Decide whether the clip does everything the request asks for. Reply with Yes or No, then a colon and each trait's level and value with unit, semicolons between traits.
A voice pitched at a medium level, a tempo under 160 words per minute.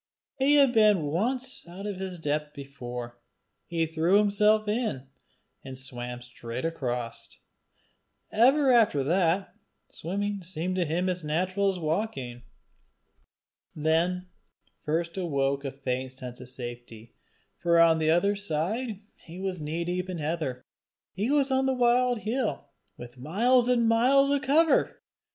Yes: medium, 175 Hz; average, 140 wpm